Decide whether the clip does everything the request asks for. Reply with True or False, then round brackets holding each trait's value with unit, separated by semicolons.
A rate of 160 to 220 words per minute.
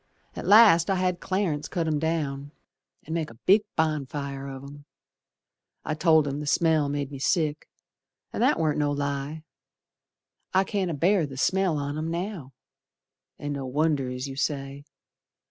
True (165 wpm)